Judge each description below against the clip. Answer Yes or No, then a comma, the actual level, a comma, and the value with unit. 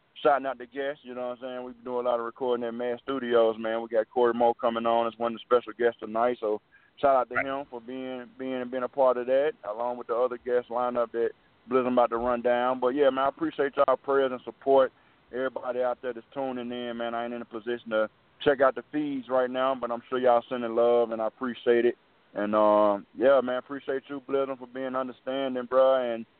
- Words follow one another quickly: Yes, fast, 250 wpm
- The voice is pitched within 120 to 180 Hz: Yes, low, 125 Hz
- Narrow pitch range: Yes, narrow, 1.8 semitones